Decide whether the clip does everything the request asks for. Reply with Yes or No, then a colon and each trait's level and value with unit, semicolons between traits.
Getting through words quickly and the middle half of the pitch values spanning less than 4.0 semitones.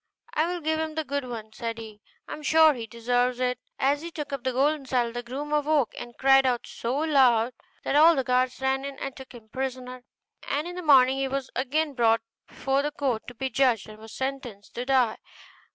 Yes: fast, 225 wpm; average, 2.9 semitones